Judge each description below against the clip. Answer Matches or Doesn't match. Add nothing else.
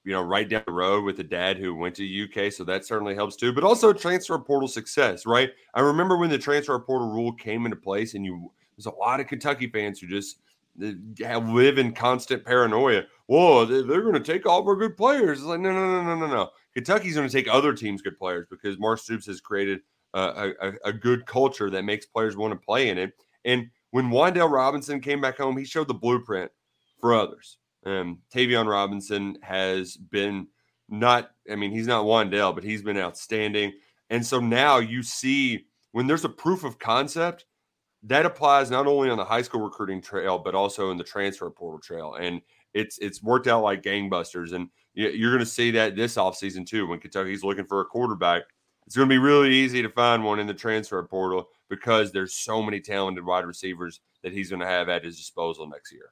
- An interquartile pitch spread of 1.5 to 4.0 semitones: Doesn't match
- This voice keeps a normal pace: Doesn't match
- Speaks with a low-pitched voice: Matches